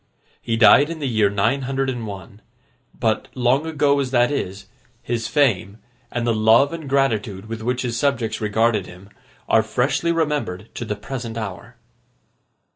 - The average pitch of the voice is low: Yes, low, 115 Hz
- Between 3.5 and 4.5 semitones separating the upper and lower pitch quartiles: Yes, average, 3.9 semitones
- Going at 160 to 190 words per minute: Yes, average, 165 wpm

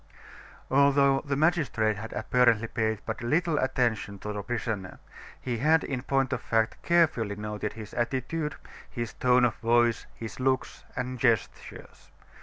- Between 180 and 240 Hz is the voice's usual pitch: No, low, 120 Hz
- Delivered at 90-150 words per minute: Yes, average, 145 wpm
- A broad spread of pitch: No, average, 3.6 semitones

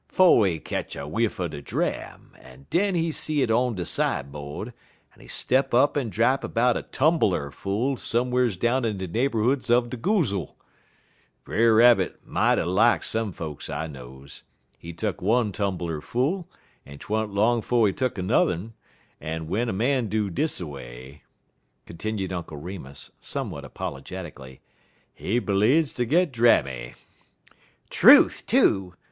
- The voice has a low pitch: Yes, low, 105 Hz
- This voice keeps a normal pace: Yes, average, 160 wpm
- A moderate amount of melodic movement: No, wide, 6.8 semitones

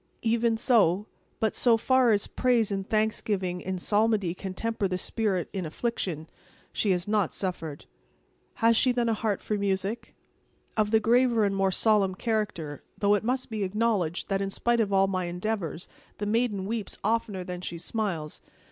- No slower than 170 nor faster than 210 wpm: Yes, average, 175 wpm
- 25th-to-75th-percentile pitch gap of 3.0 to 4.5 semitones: Yes, average, 3.3 semitones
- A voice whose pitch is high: Yes, high, 205 Hz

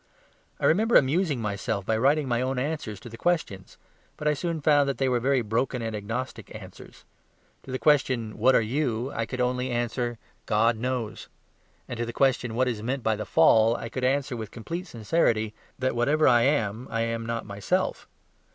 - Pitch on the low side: Yes, low, 125 Hz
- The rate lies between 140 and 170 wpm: No, average, 195 wpm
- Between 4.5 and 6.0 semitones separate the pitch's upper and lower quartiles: No, average, 3.3 semitones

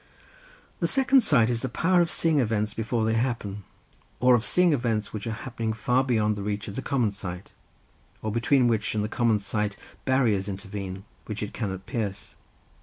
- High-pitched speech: No, low, 110 Hz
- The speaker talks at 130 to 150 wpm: No, average, 185 wpm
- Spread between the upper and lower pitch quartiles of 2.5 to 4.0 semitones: Yes, average, 3.3 semitones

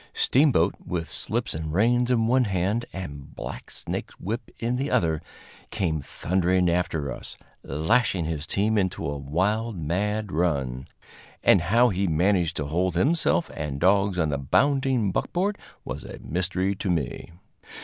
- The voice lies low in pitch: Yes, very low, 95 Hz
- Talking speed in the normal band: Yes, average, 150 wpm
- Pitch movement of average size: No, wide, 5.8 semitones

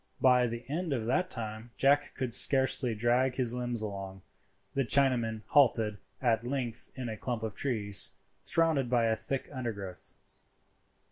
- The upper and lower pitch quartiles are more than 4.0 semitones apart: No, average, 3.1 semitones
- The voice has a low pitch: Yes, low, 120 Hz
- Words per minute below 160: Yes, average, 150 wpm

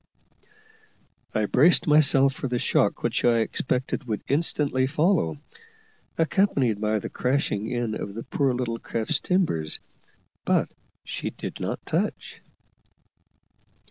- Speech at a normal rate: No, slow, 120 wpm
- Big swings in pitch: No, average, 5.0 semitones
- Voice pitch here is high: No, low, 125 Hz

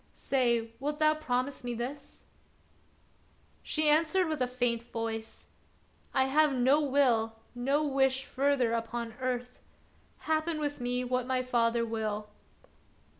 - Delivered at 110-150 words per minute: Yes, average, 140 wpm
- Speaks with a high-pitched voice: Yes, very high, 255 Hz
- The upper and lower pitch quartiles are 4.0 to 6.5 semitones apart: No, average, 3.3 semitones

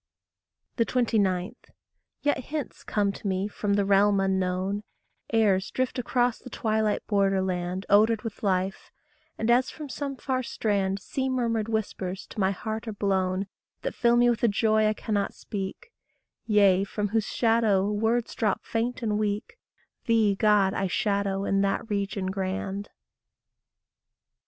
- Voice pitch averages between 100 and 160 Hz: No, high, 205 Hz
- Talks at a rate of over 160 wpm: No, average, 145 wpm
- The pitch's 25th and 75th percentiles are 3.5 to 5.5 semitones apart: No, average, 2.7 semitones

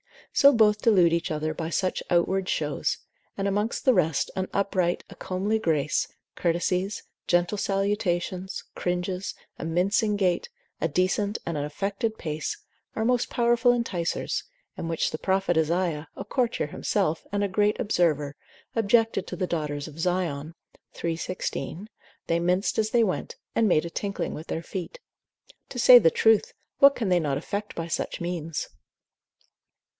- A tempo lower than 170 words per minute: Yes, average, 160 wpm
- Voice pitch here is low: No, medium, 185 Hz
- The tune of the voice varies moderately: Yes, average, 3.9 semitones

